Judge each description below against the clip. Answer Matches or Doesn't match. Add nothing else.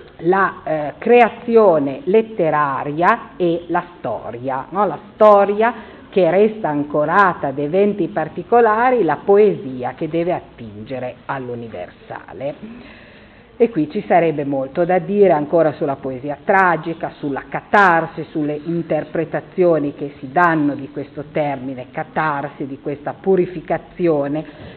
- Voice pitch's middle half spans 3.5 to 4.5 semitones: Doesn't match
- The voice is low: Doesn't match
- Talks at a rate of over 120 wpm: Doesn't match